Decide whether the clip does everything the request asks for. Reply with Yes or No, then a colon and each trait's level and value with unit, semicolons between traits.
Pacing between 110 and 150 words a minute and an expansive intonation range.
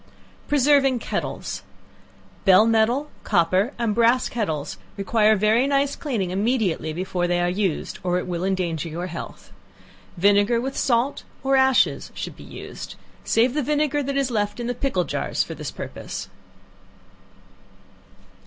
Yes: average, 145 wpm; wide, 6.2 semitones